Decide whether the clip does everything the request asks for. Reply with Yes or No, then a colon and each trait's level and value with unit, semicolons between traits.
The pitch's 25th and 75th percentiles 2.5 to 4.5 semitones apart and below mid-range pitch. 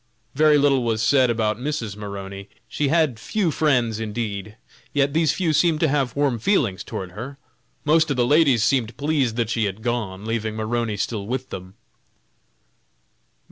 No: average, 5.1 semitones; low, 120 Hz